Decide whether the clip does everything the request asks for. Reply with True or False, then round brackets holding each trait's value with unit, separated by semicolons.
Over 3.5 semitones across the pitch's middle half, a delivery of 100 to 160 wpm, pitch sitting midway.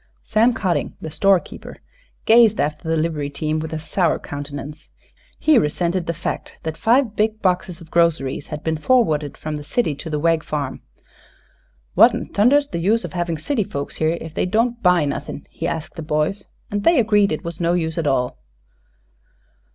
False (5.1 semitones; 180 wpm; 165 Hz)